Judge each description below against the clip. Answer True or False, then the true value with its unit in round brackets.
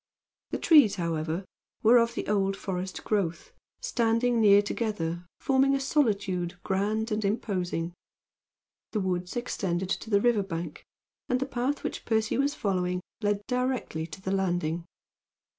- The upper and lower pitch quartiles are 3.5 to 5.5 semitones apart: True (4.5 semitones)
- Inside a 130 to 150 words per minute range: True (140 wpm)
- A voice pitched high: True (200 Hz)